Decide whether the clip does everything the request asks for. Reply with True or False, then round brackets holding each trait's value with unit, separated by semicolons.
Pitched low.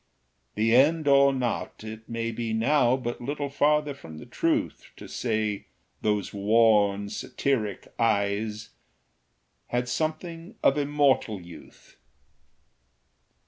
True (115 Hz)